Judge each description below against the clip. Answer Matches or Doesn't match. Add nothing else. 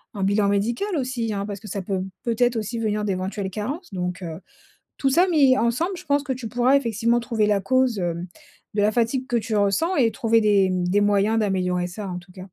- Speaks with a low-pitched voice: Doesn't match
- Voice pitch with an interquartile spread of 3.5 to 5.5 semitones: Matches